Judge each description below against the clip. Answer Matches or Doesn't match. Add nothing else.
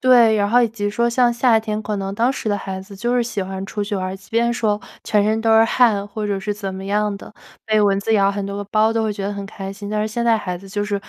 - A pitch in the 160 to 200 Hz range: Doesn't match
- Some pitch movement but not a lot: Doesn't match